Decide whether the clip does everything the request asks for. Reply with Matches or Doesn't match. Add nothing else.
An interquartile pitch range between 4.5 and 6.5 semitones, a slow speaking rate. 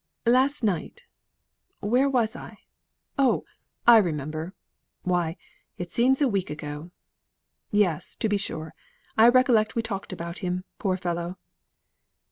Matches